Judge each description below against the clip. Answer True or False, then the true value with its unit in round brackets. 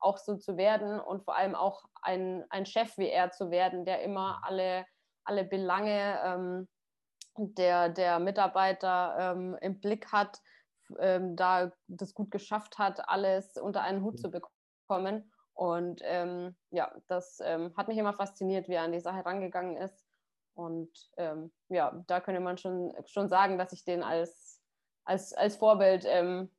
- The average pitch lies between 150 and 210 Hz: True (185 Hz)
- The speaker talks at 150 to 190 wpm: True (165 wpm)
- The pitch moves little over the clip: True (1.5 semitones)